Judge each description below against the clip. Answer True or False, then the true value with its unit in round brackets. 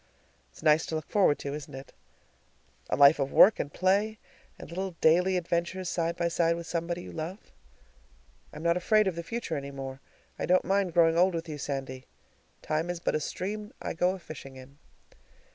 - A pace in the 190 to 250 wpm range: True (195 wpm)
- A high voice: False (170 Hz)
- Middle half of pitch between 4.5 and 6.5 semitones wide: False (3.6 semitones)